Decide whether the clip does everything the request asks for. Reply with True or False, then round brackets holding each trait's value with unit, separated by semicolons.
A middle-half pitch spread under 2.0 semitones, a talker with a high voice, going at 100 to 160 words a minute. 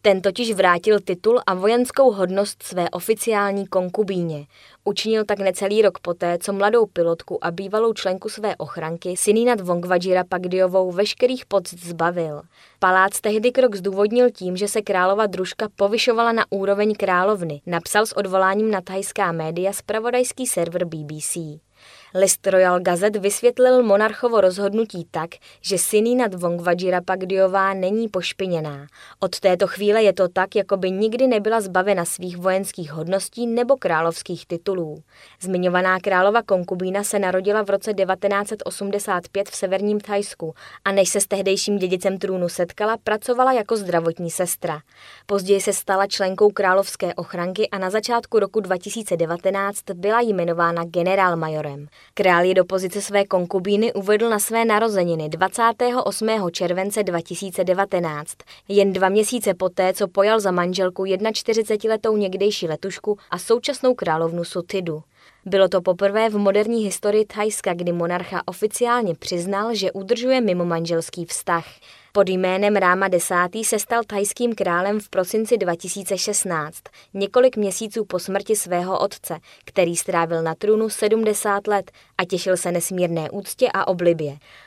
False (2.9 semitones; 195 Hz; 135 wpm)